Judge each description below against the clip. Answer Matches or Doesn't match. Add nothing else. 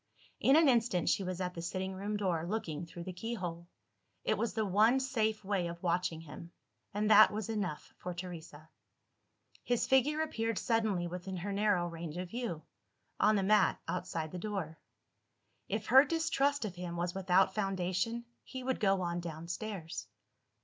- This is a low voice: Doesn't match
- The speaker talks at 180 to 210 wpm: Doesn't match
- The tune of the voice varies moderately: Matches